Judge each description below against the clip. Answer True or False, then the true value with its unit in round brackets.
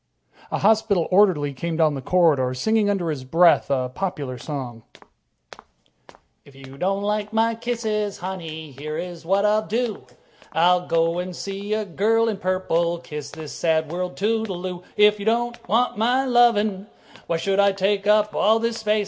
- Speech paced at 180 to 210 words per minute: False (165 wpm)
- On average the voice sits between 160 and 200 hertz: True (190 Hz)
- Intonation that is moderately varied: True (4.6 semitones)